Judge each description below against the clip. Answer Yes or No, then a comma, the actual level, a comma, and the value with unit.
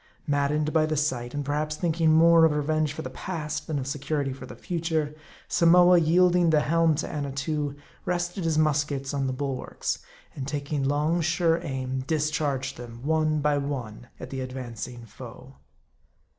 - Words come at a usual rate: Yes, average, 170 wpm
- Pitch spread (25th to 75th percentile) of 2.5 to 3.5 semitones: Yes, average, 2.8 semitones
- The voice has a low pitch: No, medium, 150 Hz